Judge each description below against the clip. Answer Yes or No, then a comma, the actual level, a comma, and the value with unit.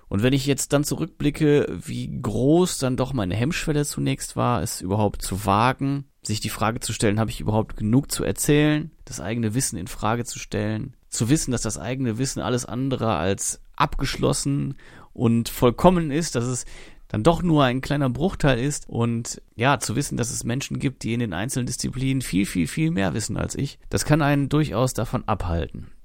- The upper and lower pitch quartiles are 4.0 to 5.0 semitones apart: Yes, average, 4.6 semitones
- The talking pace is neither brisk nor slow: No, fast, 195 wpm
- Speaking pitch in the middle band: No, low, 125 Hz